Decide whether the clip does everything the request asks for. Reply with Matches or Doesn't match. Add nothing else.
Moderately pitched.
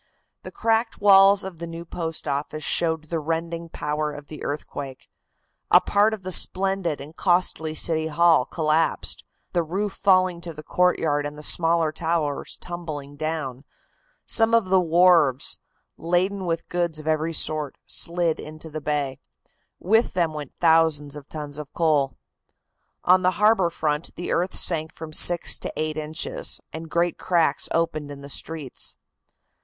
Matches